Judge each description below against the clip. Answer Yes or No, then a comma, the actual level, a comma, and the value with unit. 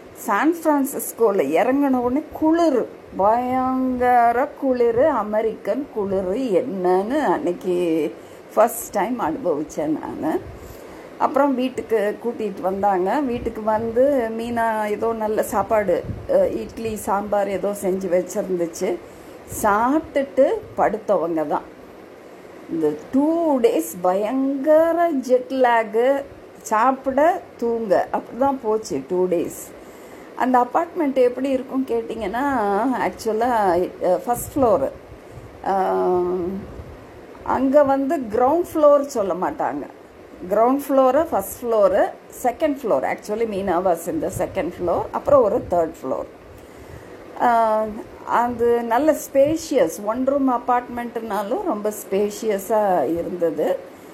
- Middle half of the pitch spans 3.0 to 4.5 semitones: No, average, 5.1 semitones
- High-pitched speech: Yes, high, 235 Hz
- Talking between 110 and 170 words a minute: No, average, 90 wpm